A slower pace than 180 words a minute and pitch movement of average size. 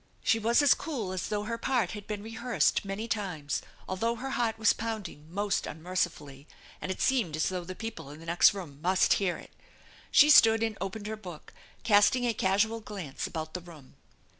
No: average, 200 wpm; average, 4.3 semitones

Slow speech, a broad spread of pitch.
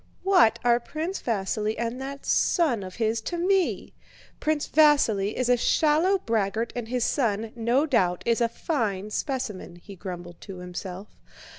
No: average, 155 wpm; wide, 6.0 semitones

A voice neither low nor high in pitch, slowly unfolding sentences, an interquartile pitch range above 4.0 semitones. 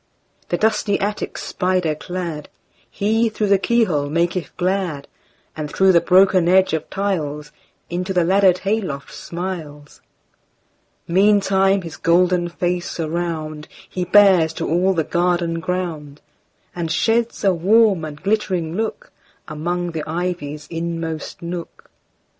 No: medium, 175 Hz; slow, 110 wpm; average, 2.9 semitones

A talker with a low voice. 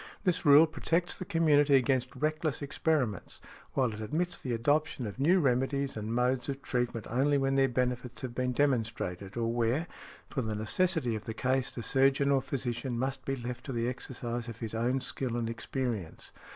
Yes: low, 130 Hz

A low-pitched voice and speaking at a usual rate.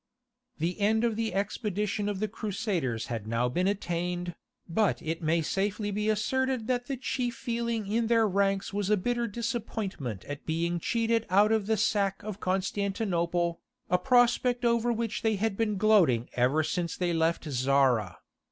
No: high, 200 Hz; average, 165 wpm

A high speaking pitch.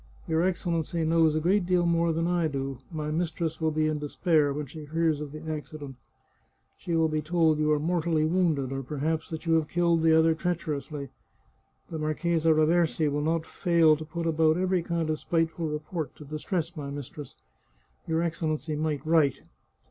No: medium, 160 Hz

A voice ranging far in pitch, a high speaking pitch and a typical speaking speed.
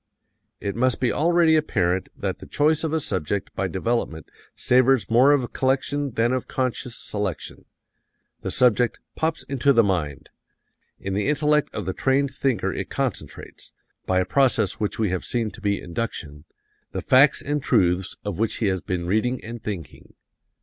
No: wide, 5.9 semitones; low, 115 Hz; average, 170 wpm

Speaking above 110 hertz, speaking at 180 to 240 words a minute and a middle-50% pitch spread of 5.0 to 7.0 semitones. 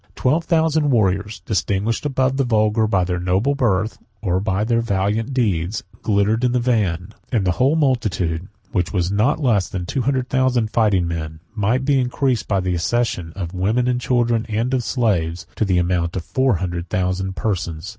No: low, 105 Hz; average, 185 wpm; wide, 5.4 semitones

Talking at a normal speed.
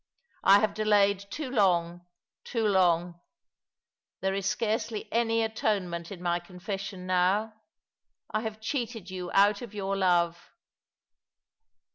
No: slow, 120 wpm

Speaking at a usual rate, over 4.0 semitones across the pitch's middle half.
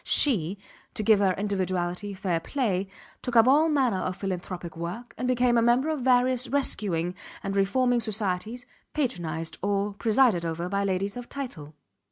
Yes: average, 160 wpm; average, 5.2 semitones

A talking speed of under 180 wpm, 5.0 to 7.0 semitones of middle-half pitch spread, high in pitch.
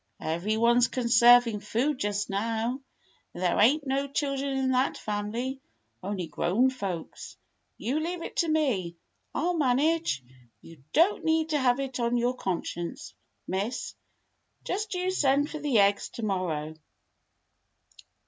Yes: average, 140 wpm; wide, 5.6 semitones; high, 245 Hz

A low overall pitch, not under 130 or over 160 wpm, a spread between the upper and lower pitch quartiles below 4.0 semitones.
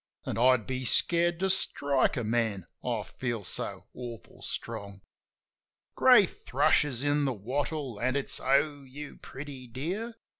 Yes: low, 130 Hz; average, 145 wpm; average, 3.6 semitones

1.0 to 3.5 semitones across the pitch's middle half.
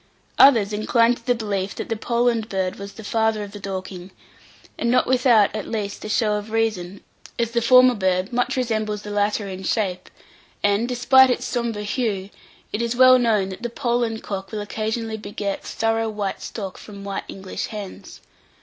Yes: average, 2.8 semitones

